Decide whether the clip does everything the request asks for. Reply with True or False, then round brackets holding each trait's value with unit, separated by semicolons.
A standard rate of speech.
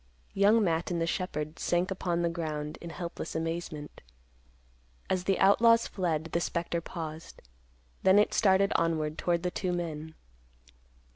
True (145 wpm)